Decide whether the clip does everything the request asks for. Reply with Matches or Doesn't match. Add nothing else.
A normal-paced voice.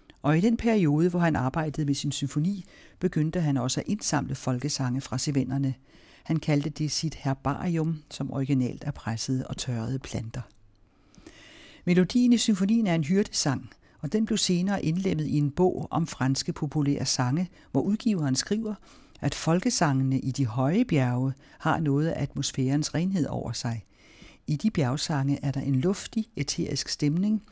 Matches